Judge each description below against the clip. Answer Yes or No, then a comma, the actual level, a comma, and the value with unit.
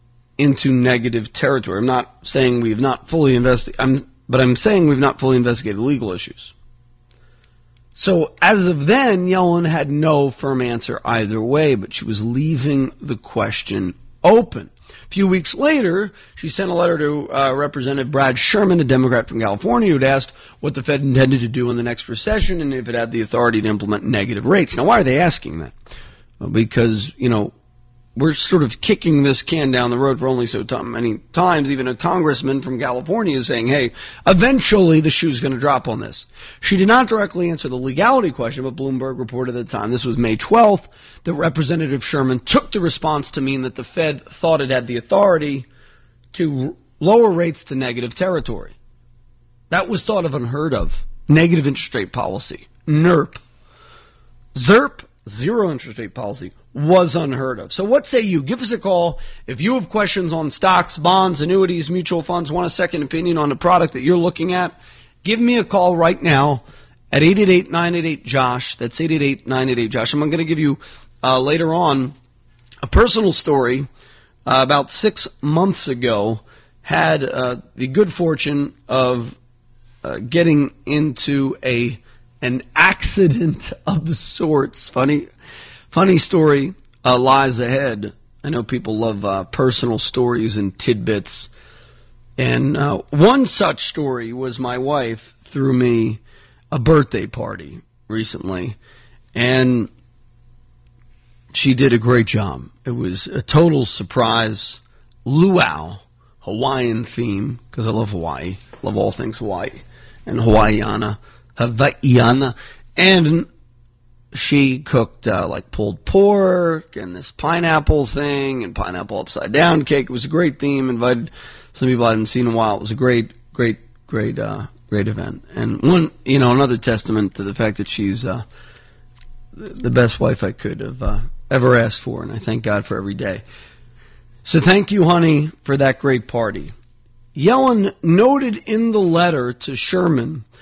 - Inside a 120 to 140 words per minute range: No, average, 165 wpm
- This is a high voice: No, low, 130 Hz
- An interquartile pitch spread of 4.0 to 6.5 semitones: Yes, average, 5.3 semitones